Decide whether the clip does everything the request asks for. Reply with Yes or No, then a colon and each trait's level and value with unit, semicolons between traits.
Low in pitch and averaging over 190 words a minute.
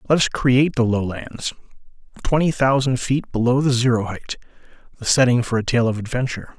No: low, 125 Hz; average, 155 wpm